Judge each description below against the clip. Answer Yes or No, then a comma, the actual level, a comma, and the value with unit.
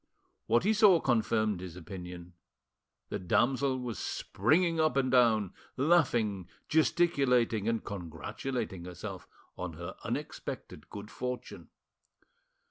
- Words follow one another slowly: Yes, slow, 110 wpm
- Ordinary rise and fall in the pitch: No, wide, 6.0 semitones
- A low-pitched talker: Yes, low, 115 Hz